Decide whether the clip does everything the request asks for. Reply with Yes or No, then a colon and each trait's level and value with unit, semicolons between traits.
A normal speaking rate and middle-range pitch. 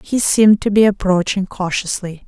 No: average, 160 wpm; high, 195 Hz